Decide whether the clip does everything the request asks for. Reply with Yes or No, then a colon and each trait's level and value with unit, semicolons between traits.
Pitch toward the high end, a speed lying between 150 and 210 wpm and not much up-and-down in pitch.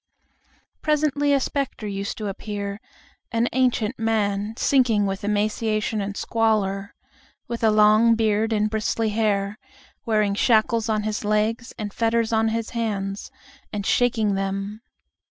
No: high, 215 Hz; slow, 135 wpm; narrow, 1.8 semitones